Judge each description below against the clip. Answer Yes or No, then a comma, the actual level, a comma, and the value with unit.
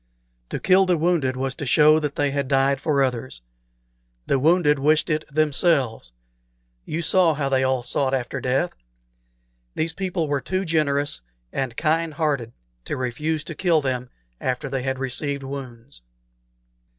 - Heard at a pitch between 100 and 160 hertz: Yes, medium, 140 Hz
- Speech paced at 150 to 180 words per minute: Yes, average, 155 wpm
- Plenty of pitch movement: No, average, 3.2 semitones